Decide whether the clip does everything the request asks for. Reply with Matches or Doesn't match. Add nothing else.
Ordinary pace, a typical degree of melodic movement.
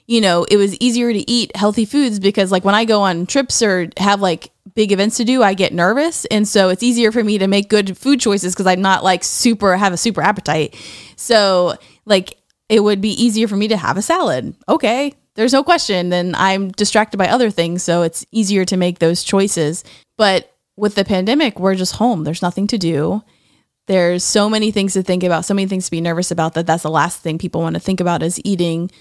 Doesn't match